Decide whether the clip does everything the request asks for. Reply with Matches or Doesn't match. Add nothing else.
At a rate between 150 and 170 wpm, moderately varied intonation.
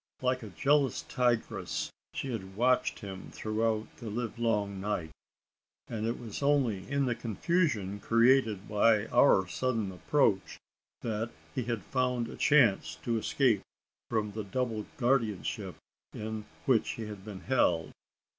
Doesn't match